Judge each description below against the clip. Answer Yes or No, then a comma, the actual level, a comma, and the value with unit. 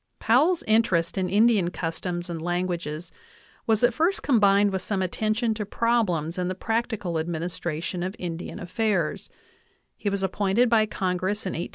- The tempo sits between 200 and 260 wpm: No, average, 155 wpm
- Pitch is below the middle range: No, high, 190 Hz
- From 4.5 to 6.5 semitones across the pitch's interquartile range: No, average, 4.0 semitones